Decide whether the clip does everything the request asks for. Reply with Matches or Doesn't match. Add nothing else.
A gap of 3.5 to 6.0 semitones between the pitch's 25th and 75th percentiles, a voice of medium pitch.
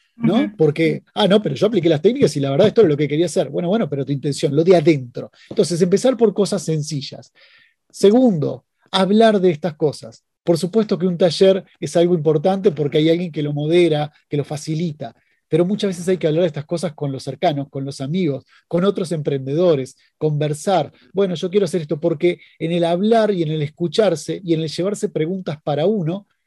Matches